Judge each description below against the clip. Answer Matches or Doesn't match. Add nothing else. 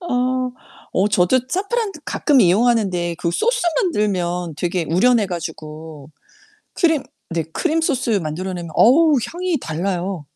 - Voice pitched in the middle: Doesn't match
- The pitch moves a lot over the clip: Matches